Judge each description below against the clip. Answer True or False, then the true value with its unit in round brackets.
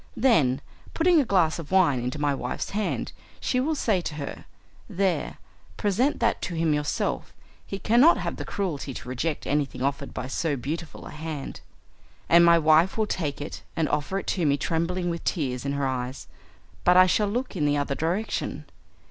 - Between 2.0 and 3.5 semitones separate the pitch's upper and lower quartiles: False (5.2 semitones)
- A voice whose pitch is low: False (165 Hz)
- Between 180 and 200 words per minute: True (190 wpm)